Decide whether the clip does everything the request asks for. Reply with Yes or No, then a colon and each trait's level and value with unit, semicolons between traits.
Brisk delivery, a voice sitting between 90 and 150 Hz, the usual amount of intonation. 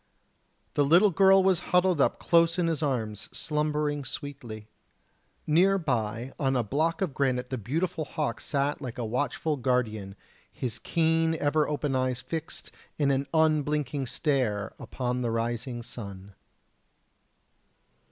No: slow, 135 wpm; medium, 140 Hz; average, 4.6 semitones